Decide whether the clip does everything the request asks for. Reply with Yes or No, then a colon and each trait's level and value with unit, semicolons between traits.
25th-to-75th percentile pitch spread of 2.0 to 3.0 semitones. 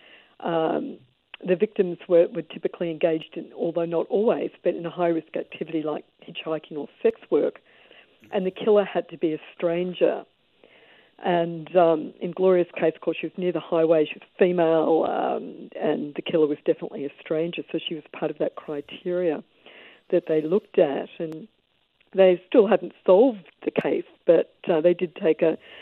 Yes: narrow, 2.5 semitones